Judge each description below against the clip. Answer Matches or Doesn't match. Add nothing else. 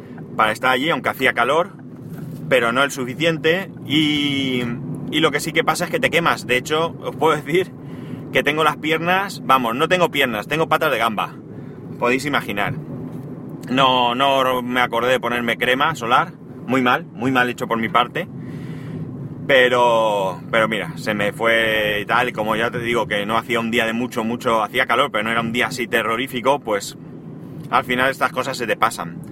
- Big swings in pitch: Doesn't match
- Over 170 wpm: Matches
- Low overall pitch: Matches